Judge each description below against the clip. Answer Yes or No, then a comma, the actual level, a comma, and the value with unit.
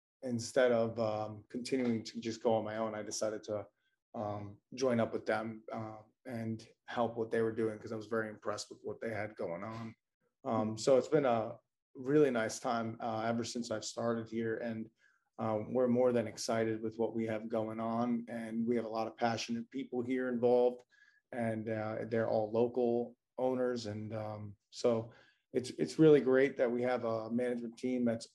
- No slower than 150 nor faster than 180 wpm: No, average, 195 wpm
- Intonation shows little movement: Yes, narrow, 1.7 semitones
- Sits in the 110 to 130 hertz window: Yes, low, 115 Hz